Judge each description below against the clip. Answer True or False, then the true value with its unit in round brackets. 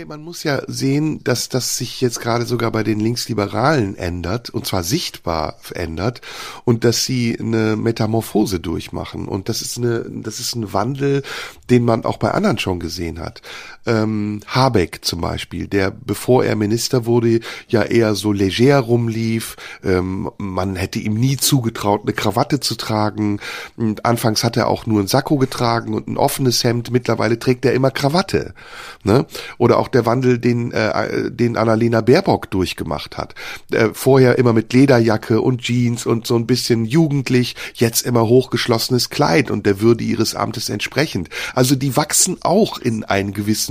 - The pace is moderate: True (160 wpm)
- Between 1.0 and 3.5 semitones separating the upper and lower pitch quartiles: True (2.8 semitones)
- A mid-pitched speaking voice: False (115 Hz)